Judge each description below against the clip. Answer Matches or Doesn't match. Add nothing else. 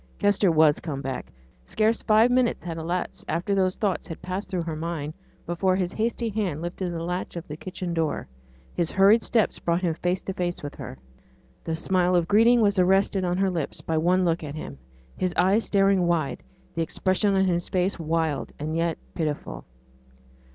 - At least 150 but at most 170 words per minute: Doesn't match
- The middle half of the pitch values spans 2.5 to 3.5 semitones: Matches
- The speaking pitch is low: Doesn't match